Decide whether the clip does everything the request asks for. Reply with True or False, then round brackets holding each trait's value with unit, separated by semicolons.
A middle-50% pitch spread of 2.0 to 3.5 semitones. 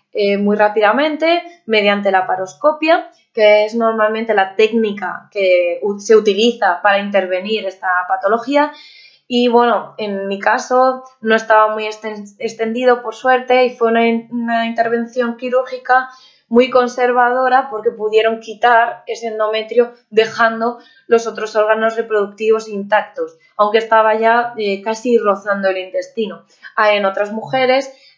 True (2.8 semitones)